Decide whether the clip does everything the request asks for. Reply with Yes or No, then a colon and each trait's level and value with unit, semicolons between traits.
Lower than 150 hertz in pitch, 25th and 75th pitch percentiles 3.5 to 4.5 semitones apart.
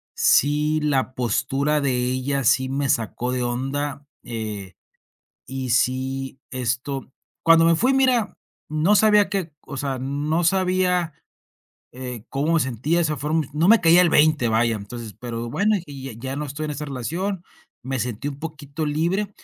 Yes: medium, 140 Hz; average, 4.2 semitones